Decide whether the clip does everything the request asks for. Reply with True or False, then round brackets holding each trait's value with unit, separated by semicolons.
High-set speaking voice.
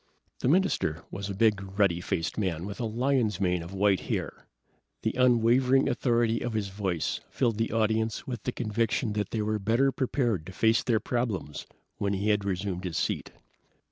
False (110 Hz)